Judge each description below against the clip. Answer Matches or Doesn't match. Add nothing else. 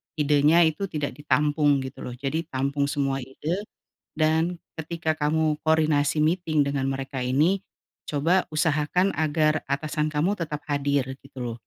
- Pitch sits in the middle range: Matches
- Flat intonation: Matches